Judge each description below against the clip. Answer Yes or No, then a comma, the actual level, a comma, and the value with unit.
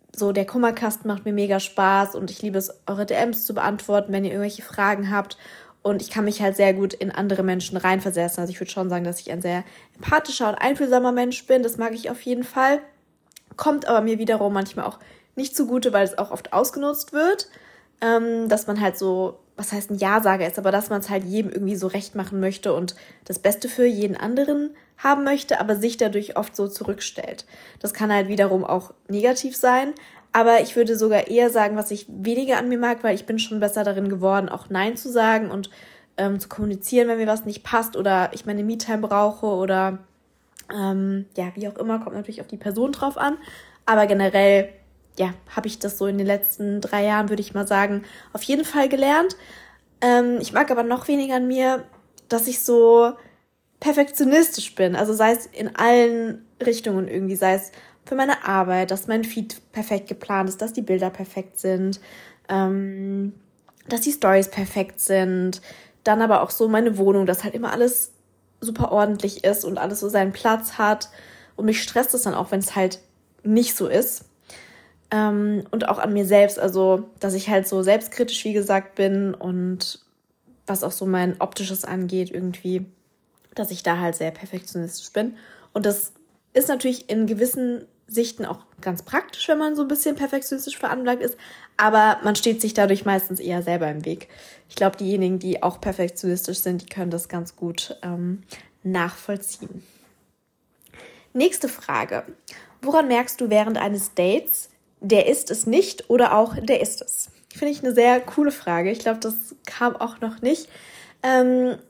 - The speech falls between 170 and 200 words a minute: Yes, fast, 190 wpm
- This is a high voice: Yes, high, 210 Hz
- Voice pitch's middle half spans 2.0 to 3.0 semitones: No, average, 3.6 semitones